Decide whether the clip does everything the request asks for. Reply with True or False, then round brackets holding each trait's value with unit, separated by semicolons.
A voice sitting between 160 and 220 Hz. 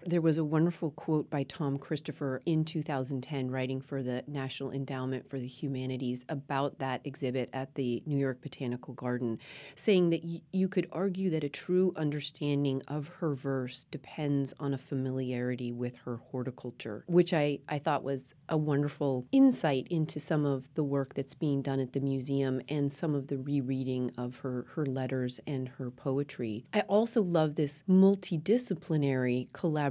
False (140 Hz)